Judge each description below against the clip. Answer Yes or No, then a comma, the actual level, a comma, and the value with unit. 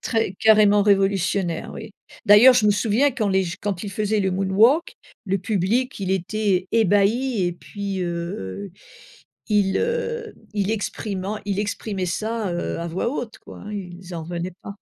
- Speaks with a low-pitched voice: No, high, 200 Hz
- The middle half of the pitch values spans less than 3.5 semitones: Yes, average, 2.8 semitones